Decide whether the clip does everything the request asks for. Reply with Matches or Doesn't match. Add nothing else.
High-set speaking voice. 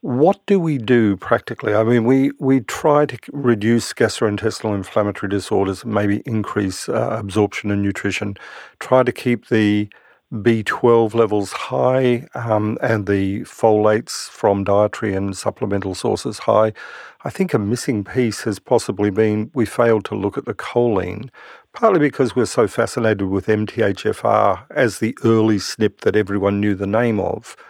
Doesn't match